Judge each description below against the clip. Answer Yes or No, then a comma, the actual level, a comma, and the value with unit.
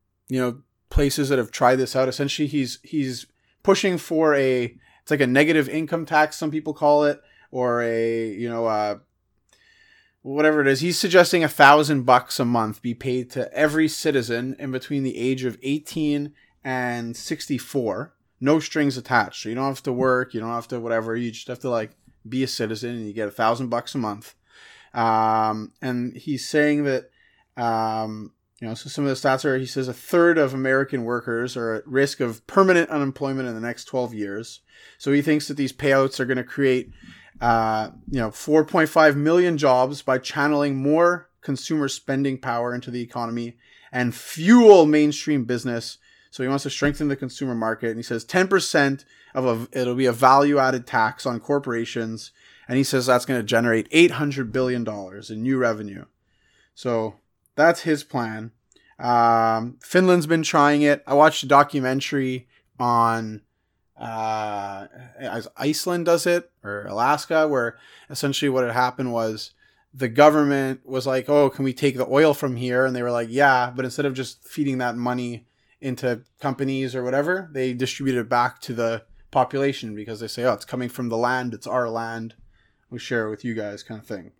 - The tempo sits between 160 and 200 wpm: Yes, average, 185 wpm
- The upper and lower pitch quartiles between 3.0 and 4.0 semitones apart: Yes, average, 3.5 semitones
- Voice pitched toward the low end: Yes, low, 130 Hz